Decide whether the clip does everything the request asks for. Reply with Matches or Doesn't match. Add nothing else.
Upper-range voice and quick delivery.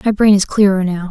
Matches